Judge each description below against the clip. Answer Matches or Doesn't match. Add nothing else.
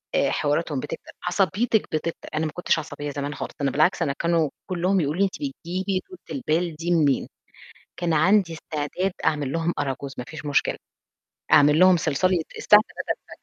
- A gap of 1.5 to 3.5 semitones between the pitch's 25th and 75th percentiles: Doesn't match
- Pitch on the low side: Doesn't match